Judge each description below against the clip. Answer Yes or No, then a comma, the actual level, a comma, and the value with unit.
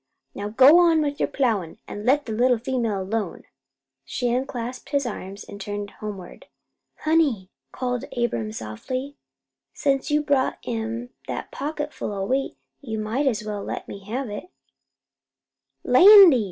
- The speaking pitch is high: Yes, high, 240 Hz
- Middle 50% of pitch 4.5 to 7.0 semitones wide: Yes, average, 5.0 semitones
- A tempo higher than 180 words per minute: No, average, 150 wpm